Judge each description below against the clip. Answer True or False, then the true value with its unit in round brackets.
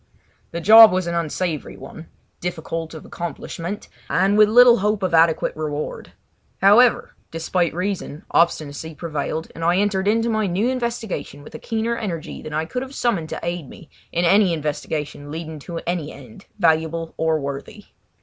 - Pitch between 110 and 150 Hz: False (170 Hz)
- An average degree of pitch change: True (4.5 semitones)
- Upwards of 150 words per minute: True (165 wpm)